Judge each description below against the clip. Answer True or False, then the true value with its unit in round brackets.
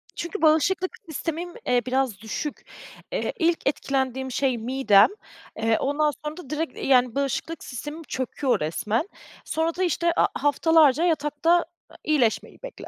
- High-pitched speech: True (290 Hz)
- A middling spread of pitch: True (4.2 semitones)